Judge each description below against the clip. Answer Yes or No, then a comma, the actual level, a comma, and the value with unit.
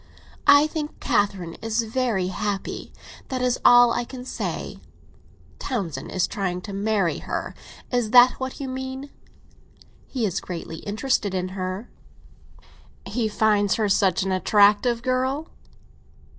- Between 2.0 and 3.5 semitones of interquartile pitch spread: No, average, 4.8 semitones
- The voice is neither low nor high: No, high, 220 Hz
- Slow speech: Yes, slow, 130 wpm